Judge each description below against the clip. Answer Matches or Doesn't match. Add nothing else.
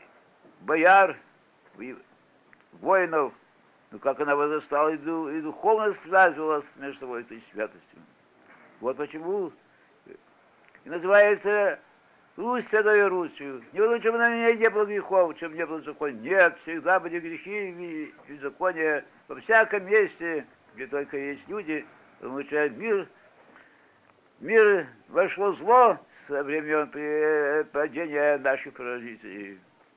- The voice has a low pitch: Doesn't match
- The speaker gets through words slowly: Matches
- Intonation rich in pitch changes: Matches